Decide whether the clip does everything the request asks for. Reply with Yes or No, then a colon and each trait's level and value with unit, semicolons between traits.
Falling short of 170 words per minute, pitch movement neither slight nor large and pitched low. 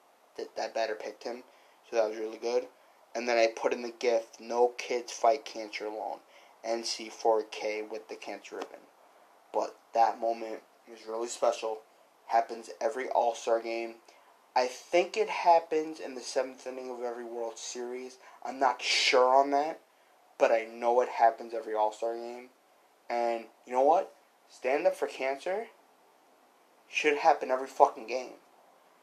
No: average, 155 wpm; narrow, 2.1 semitones; low, 115 Hz